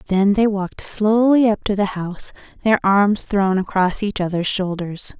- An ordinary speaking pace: Yes, average, 175 wpm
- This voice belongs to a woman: Yes, female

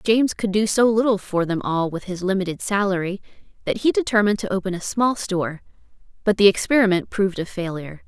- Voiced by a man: No, female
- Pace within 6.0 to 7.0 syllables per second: Yes, 6.2 syllables/s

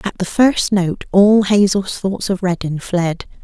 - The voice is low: No, high, 190 Hz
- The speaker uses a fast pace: No, average, 175 wpm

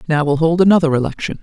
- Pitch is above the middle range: No, medium, 160 Hz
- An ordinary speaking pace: No, fast, 210 wpm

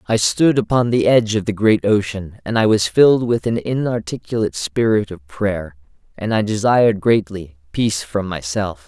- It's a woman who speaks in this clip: No, male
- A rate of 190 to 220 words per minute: No, average, 170 wpm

